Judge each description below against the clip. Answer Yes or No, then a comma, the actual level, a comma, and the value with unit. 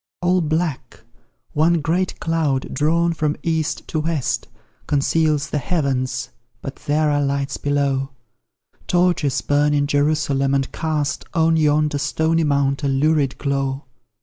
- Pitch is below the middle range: No, medium, 150 Hz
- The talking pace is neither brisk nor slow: No, slow, 130 wpm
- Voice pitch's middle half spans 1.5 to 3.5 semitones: Yes, narrow, 2.5 semitones